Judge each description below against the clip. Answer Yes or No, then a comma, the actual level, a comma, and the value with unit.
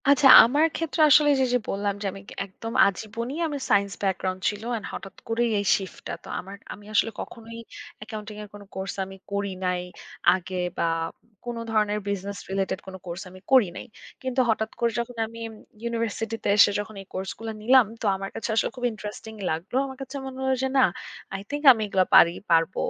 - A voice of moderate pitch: No, high, 215 Hz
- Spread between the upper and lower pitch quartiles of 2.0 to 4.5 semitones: Yes, average, 3.4 semitones